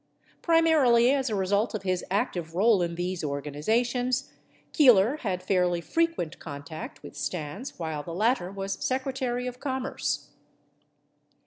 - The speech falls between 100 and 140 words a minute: Yes, slow, 135 wpm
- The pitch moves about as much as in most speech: No, wide, 6.4 semitones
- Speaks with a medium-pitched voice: No, high, 205 Hz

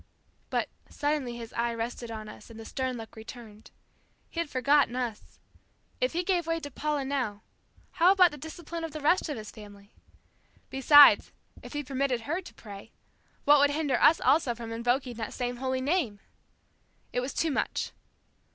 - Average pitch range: Yes, average, 4.5 semitones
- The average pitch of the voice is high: Yes, very high, 260 Hz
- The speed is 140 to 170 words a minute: No, average, 180 wpm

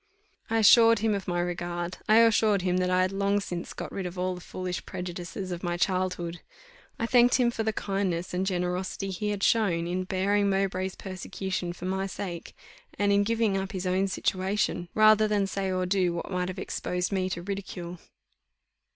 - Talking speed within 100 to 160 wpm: No, average, 195 wpm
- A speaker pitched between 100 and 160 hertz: No, high, 190 Hz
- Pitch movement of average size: No, narrow, 2.0 semitones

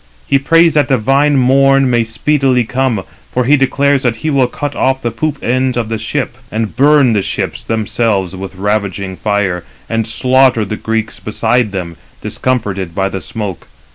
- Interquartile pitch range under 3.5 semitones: No, average, 4.1 semitones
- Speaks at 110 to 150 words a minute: No, average, 175 wpm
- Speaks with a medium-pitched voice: No, low, 120 Hz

